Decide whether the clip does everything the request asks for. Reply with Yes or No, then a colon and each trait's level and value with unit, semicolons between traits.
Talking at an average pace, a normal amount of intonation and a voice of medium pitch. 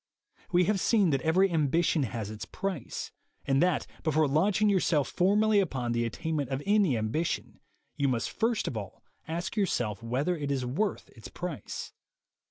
No: average, 165 wpm; wide, 6.4 semitones; medium, 155 Hz